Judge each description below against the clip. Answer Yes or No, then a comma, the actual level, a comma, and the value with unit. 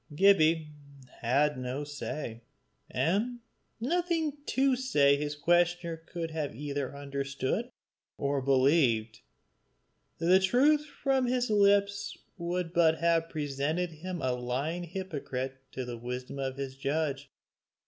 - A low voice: No, medium, 155 Hz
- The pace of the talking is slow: Yes, slow, 120 wpm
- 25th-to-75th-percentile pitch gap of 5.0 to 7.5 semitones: Yes, wide, 5.5 semitones